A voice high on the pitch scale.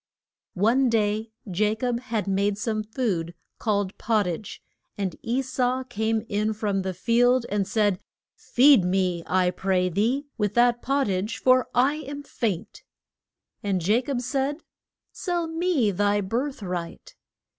Yes: high, 220 Hz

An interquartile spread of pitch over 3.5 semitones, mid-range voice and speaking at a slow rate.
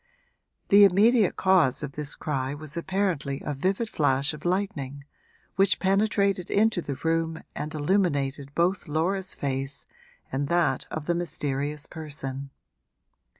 Yes: average, 5.1 semitones; medium, 160 Hz; slow, 130 wpm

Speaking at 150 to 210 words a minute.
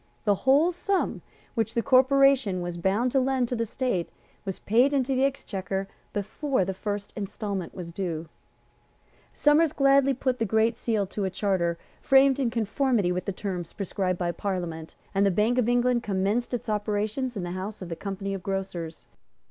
Yes: average, 180 wpm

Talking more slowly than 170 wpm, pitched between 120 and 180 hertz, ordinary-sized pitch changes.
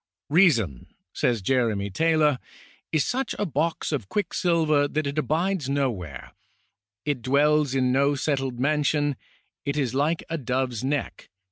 Yes: average, 160 wpm; medium, 140 Hz; average, 3.4 semitones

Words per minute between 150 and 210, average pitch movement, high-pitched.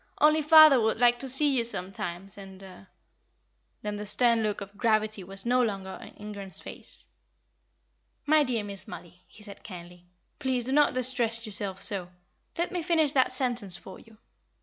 Yes: average, 170 wpm; average, 4.7 semitones; high, 220 Hz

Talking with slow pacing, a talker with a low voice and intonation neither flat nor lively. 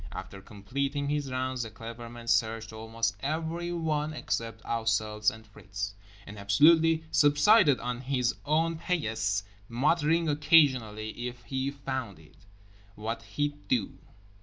Yes: slow, 125 wpm; low, 125 Hz; average, 5.0 semitones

